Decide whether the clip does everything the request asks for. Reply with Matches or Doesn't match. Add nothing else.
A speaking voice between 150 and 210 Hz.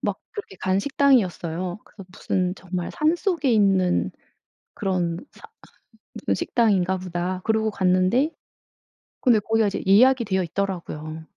Matches